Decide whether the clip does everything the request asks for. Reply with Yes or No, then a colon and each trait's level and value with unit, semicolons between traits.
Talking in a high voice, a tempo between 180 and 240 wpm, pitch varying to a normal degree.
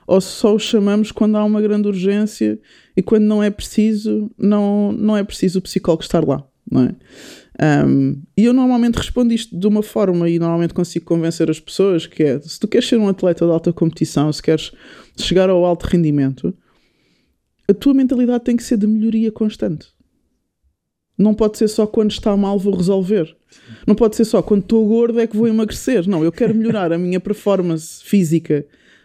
Yes: high, 200 Hz; average, 190 wpm; average, 4.5 semitones